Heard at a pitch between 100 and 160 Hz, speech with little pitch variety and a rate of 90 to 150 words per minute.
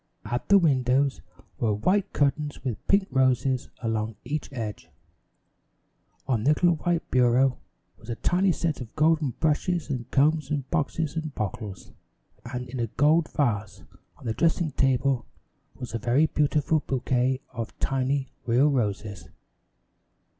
No: low, 135 Hz; average, 4.1 semitones; average, 140 wpm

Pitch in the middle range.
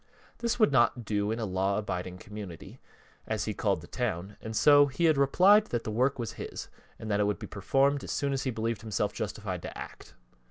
No: low, 110 Hz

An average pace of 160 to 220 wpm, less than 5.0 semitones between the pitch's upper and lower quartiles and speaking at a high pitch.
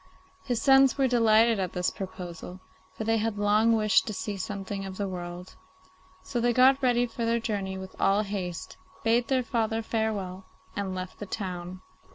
Yes: average, 180 wpm; average, 3.5 semitones; high, 210 Hz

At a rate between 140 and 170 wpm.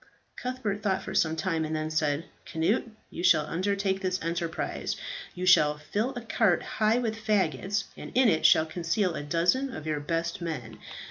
No: average, 180 wpm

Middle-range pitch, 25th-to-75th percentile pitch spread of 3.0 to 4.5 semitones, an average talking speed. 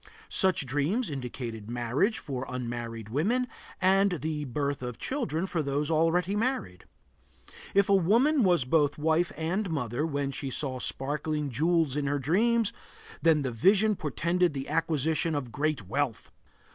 No: medium, 150 Hz; average, 5.2 semitones; average, 145 wpm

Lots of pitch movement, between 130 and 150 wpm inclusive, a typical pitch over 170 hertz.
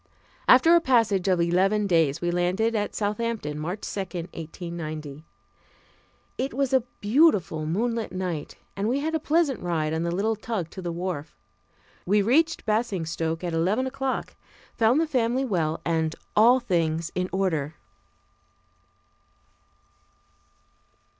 Yes: wide, 5.8 semitones; slow, 135 wpm; high, 190 Hz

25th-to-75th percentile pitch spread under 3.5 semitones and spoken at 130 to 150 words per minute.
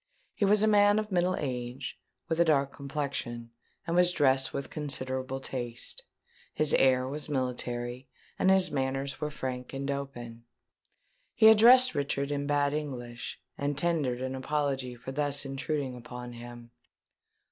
Yes: average, 3.1 semitones; average, 145 wpm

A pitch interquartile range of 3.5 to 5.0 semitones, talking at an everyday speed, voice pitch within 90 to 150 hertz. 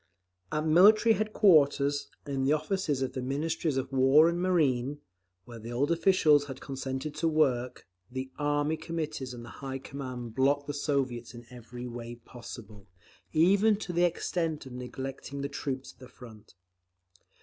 Yes: average, 3.8 semitones; average, 160 wpm; medium, 140 Hz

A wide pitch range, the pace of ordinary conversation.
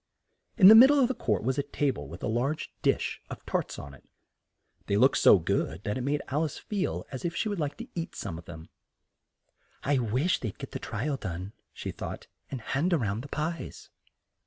No: wide, 8.1 semitones; fast, 225 wpm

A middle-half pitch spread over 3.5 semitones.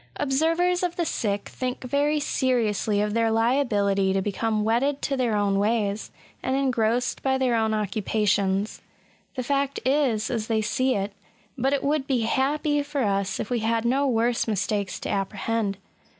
Yes: average, 4.4 semitones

